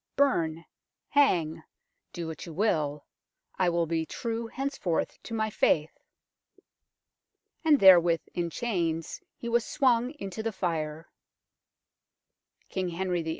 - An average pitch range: No, wide, 5.9 semitones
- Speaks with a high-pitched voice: No, medium, 180 Hz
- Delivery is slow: Yes, slow, 120 wpm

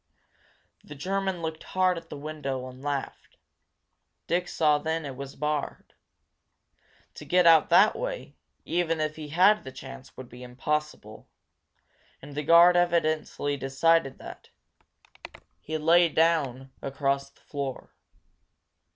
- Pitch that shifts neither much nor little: Yes, average, 3.5 semitones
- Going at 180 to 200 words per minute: No, slow, 135 wpm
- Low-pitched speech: No, medium, 155 Hz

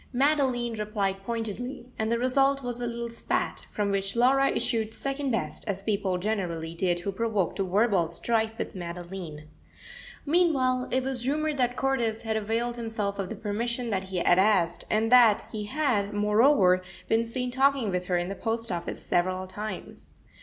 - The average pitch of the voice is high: Yes, high, 220 Hz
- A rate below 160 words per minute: No, average, 175 wpm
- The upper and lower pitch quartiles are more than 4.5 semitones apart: No, average, 4.2 semitones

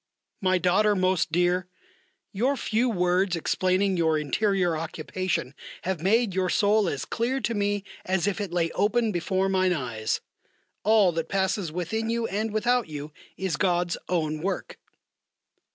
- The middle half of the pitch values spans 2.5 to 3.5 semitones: Yes, average, 3.2 semitones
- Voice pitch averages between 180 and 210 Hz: Yes, medium, 185 Hz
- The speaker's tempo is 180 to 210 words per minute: No, average, 150 wpm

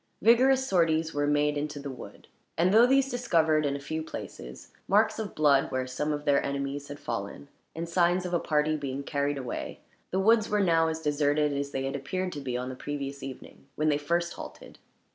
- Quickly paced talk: Yes, fast, 210 wpm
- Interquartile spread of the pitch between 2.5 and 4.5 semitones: Yes, average, 3.7 semitones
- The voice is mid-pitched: Yes, medium, 150 Hz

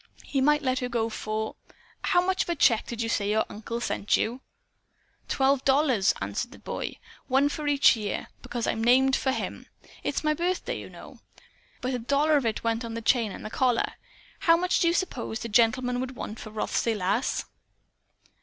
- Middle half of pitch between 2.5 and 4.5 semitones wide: Yes, average, 3.8 semitones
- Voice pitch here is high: Yes, very high, 250 Hz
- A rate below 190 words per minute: No, average, 200 wpm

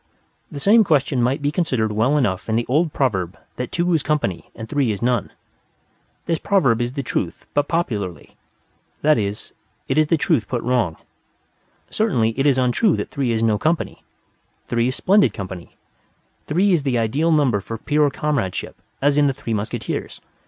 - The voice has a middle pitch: No, low, 130 Hz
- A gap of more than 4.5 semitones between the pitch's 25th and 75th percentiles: Yes, average, 5.2 semitones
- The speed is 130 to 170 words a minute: No, average, 180 wpm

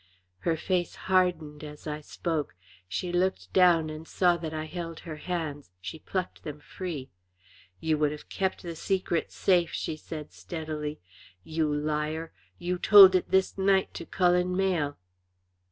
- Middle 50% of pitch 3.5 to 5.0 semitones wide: No, average, 3.0 semitones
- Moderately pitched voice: Yes, medium, 165 Hz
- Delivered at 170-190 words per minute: No, average, 155 wpm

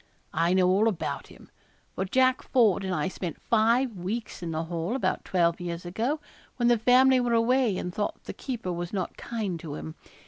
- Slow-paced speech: No, average, 200 wpm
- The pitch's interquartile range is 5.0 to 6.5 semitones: Yes, wide, 5.4 semitones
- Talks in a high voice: Yes, high, 200 Hz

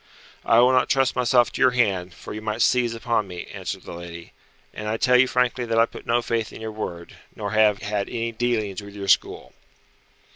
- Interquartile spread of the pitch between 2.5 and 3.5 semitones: Yes, average, 3.0 semitones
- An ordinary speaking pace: No, fast, 220 wpm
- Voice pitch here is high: No, low, 115 Hz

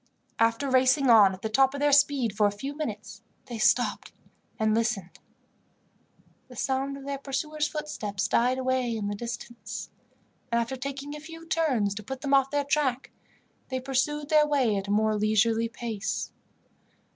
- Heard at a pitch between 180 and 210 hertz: No, very high, 255 Hz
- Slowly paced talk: No, average, 170 wpm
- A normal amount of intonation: Yes, average, 4.2 semitones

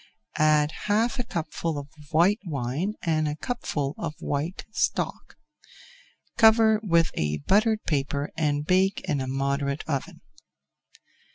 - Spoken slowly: Yes, slow, 125 wpm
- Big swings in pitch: Yes, wide, 5.8 semitones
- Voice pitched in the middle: Yes, medium, 155 Hz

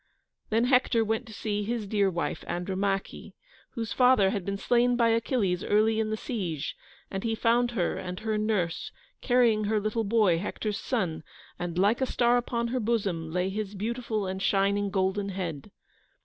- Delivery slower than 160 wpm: No, average, 175 wpm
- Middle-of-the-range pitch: No, high, 210 Hz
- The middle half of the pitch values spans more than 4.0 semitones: No, average, 3.3 semitones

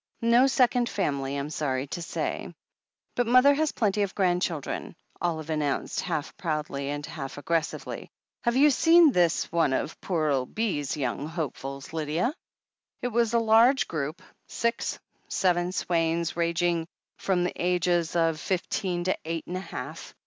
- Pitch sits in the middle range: Yes, medium, 170 Hz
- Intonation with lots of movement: Yes, wide, 5.8 semitones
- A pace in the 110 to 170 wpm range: Yes, average, 155 wpm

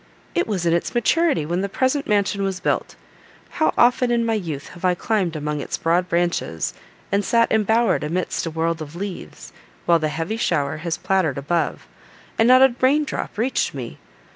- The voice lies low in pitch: No, medium, 185 Hz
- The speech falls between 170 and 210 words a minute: Yes, average, 190 wpm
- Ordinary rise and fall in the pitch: No, wide, 5.8 semitones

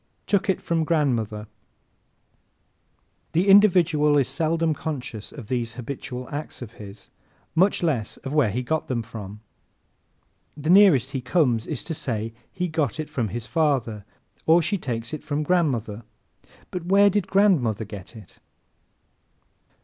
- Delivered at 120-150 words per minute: Yes, average, 145 wpm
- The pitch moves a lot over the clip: Yes, wide, 6.2 semitones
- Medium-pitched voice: Yes, medium, 145 Hz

